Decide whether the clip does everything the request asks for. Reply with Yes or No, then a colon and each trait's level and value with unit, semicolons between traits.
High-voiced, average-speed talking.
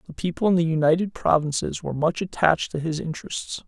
No: medium, 165 Hz; average, 195 wpm